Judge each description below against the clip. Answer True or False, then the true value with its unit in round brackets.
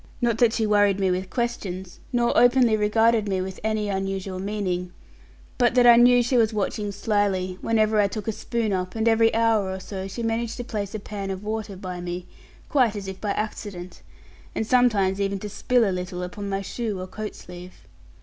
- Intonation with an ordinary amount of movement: True (3.0 semitones)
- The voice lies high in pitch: True (205 Hz)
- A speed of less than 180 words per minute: False (205 wpm)